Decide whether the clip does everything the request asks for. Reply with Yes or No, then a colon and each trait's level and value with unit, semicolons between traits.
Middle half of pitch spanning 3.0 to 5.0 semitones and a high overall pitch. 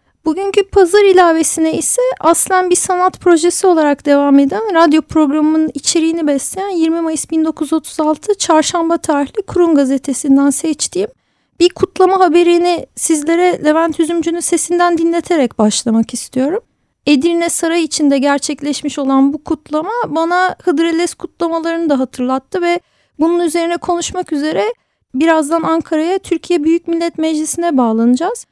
No: narrow, 2.6 semitones; very high, 330 Hz